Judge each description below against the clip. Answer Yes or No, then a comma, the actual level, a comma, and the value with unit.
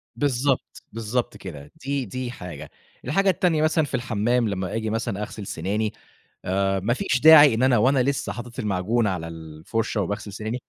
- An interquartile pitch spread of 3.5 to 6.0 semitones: Yes, average, 4.6 semitones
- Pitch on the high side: No, low, 115 Hz